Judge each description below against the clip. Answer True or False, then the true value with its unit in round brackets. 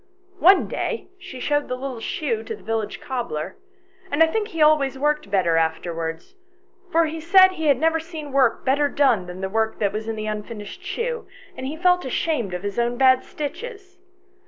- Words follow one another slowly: False (195 wpm)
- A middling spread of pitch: False (7.2 semitones)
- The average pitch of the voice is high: True (270 Hz)